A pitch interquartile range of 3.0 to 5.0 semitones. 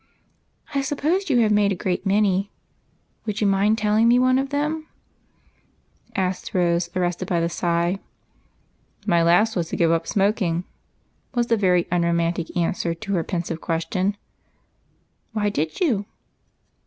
Yes: average, 4.2 semitones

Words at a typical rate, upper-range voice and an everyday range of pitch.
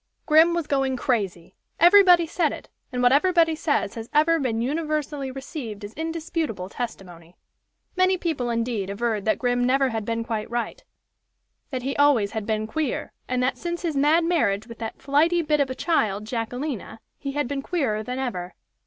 No: average, 180 wpm; very high, 260 Hz; wide, 5.7 semitones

